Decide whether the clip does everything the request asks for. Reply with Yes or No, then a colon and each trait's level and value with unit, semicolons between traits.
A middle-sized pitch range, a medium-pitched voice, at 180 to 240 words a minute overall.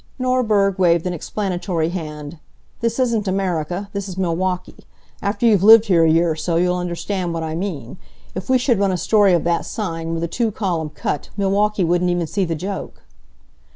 Yes: average, 3.3 semitones; medium, 180 Hz; average, 190 wpm